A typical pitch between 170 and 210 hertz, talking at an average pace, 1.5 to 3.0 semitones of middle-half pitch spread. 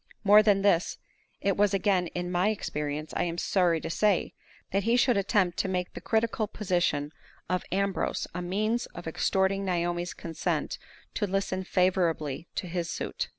Yes: medium, 185 Hz; average, 165 wpm; narrow, 2.5 semitones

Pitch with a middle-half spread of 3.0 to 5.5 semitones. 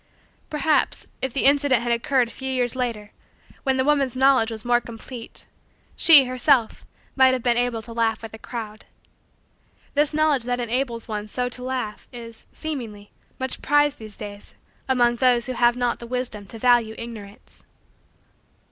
No: narrow, 2.5 semitones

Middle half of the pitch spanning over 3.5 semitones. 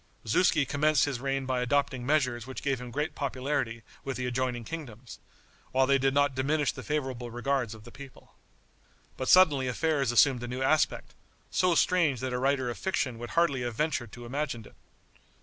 No: average, 2.8 semitones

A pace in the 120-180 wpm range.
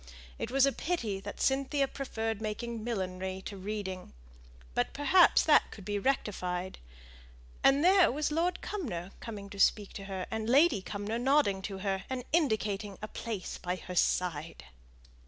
Yes: average, 155 wpm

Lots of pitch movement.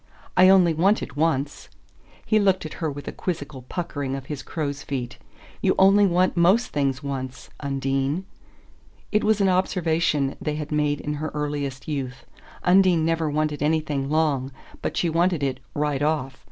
No: average, 3.7 semitones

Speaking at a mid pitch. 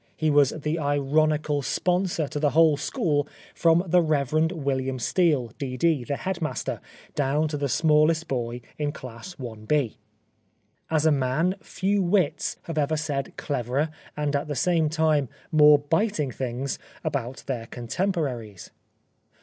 Yes: medium, 150 Hz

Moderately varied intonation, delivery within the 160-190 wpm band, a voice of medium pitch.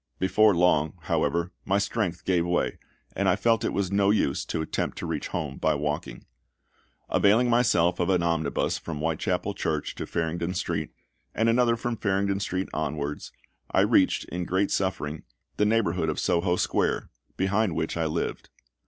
No: average, 3.7 semitones; average, 165 wpm; very low, 90 Hz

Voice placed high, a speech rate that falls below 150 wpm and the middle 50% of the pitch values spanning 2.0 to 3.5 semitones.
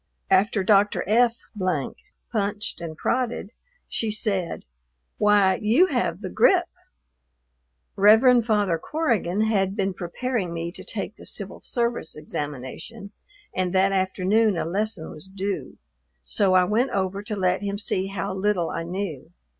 Yes: high, 200 Hz; average, 140 wpm; average, 2.9 semitones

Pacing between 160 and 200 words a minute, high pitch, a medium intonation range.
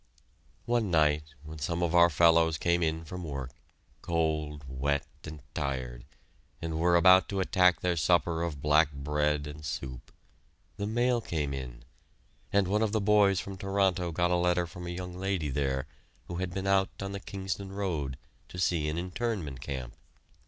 No: average, 175 wpm; very low, 85 Hz; average, 4.0 semitones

